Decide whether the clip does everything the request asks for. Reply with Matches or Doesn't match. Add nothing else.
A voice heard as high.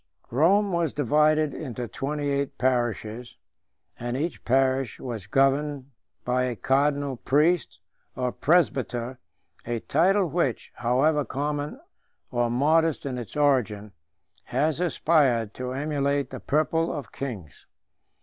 Doesn't match